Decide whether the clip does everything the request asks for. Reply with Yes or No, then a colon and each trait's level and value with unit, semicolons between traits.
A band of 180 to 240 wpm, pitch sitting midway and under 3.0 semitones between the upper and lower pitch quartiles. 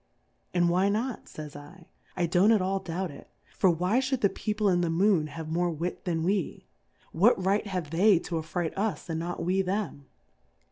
No: average, 200 wpm; medium, 180 Hz; average, 3.4 semitones